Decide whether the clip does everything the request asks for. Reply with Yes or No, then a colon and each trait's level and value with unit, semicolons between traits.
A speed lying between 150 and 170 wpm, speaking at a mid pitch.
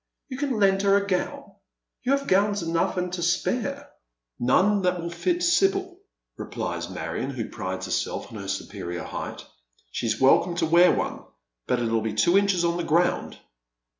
No: average, 180 wpm; medium, 180 Hz